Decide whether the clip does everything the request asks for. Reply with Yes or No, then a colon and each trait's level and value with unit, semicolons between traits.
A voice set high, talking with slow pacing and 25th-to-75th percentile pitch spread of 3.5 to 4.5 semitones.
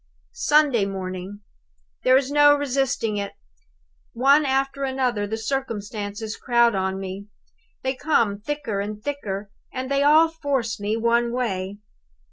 No: high, 235 Hz; slow, 130 wpm; average, 5.0 semitones